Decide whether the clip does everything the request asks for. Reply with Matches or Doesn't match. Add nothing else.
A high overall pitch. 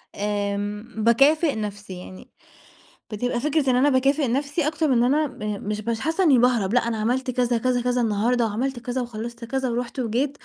Matches